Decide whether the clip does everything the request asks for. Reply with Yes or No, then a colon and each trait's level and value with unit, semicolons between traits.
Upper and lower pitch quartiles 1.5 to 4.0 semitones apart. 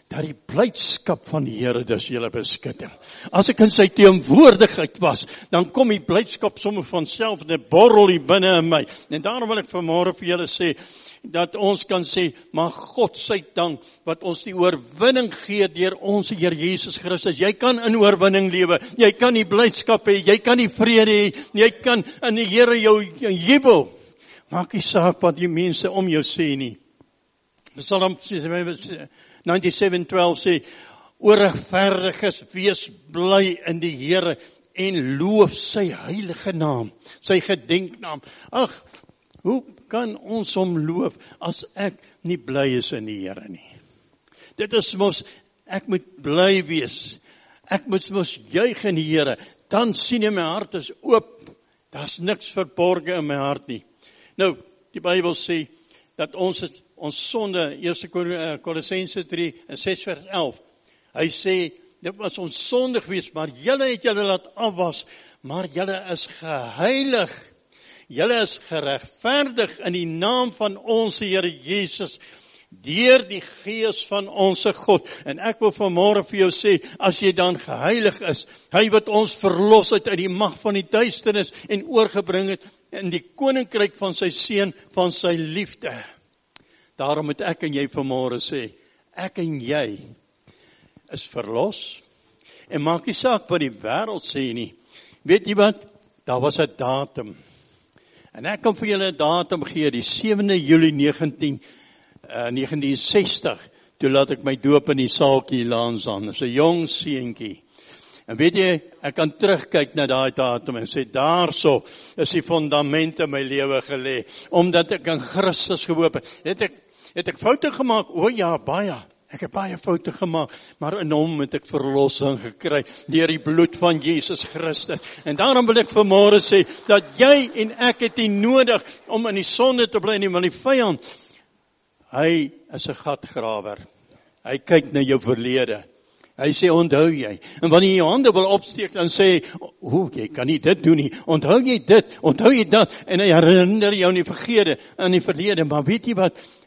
No: average, 4.6 semitones